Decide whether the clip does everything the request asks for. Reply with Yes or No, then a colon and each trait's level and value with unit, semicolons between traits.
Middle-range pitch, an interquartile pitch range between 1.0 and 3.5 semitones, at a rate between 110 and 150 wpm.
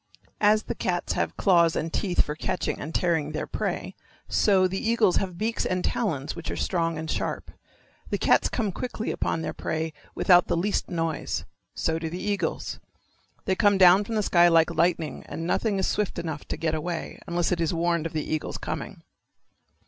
No: medium, 175 Hz; average, 2.9 semitones; average, 195 wpm